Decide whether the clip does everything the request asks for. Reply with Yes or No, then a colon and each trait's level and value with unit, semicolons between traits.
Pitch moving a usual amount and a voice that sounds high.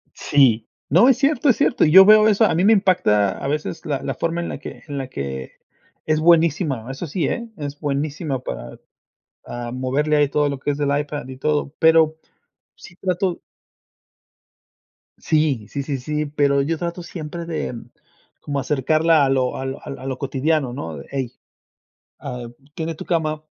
No: average, 3.7 semitones; medium, 150 Hz